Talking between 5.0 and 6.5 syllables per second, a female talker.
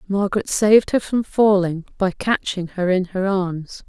No: 4.5 syllables/s; female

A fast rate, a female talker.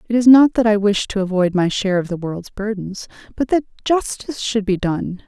Yes: fast, 230 wpm; female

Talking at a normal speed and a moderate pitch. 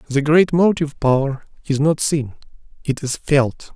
Yes: average, 160 wpm; medium, 145 Hz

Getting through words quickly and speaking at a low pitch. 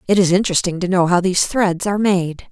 No: fast, 240 wpm; medium, 185 Hz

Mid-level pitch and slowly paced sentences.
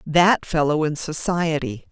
Yes: medium, 155 Hz; slow, 125 wpm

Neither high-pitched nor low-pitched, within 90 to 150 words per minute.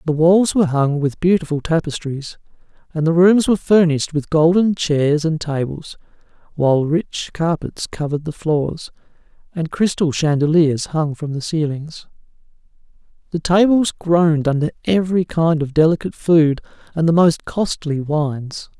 Yes: medium, 160 Hz; average, 140 wpm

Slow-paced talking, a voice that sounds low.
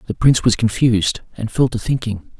No: average, 200 wpm; low, 115 Hz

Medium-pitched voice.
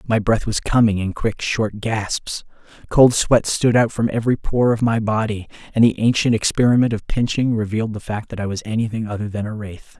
No: low, 110 Hz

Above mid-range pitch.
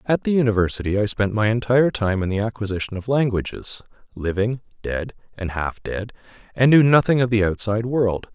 No: low, 110 Hz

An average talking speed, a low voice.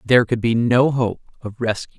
No: fast, 210 wpm; low, 120 Hz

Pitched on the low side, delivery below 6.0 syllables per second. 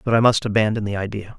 No: low, 110 Hz; 7.0 syllables/s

